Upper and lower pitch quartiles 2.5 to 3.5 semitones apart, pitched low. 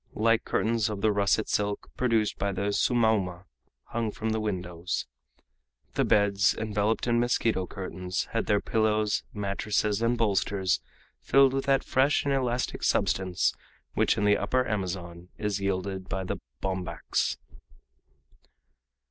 Yes: average, 3.0 semitones; low, 105 Hz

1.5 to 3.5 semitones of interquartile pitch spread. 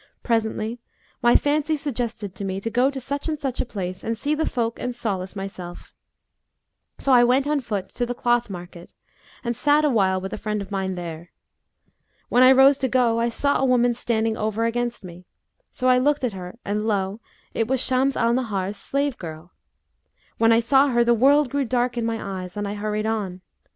No: average, 4.3 semitones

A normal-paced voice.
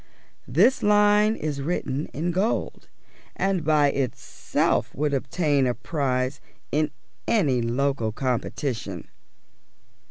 No: slow, 100 wpm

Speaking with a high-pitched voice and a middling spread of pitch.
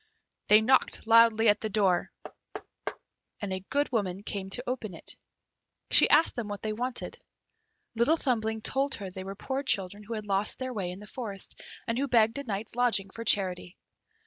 Yes: high, 220 Hz; average, 3.7 semitones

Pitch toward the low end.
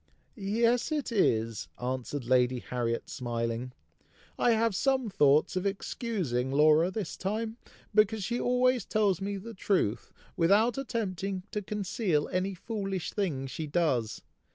No: high, 190 Hz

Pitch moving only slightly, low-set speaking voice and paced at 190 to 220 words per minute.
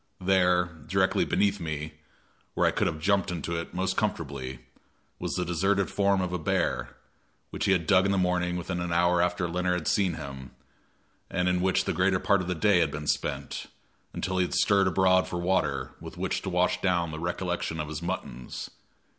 Yes: narrow, 2.0 semitones; very low, 90 Hz; average, 200 wpm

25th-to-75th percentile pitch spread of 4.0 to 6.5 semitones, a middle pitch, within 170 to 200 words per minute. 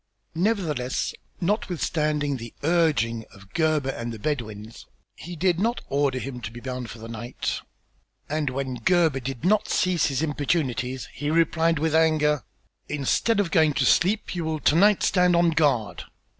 No: average, 4.9 semitones; medium, 150 Hz; average, 160 wpm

